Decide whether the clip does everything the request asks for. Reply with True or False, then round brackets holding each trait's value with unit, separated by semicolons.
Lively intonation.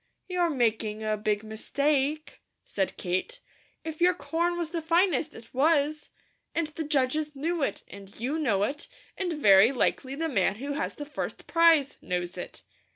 True (6.9 semitones)